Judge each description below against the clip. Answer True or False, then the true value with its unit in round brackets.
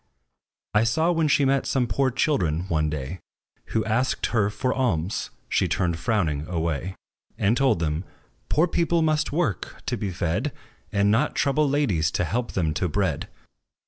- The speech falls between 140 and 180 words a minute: True (165 wpm)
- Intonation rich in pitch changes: True (8.6 semitones)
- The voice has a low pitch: True (105 Hz)